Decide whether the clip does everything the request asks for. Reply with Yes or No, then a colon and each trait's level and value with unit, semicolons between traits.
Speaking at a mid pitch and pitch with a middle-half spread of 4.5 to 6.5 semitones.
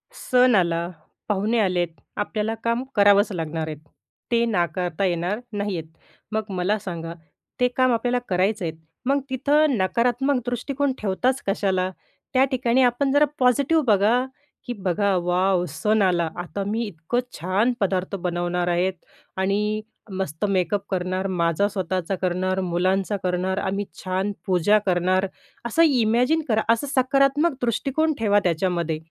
No: high, 200 Hz; average, 4.8 semitones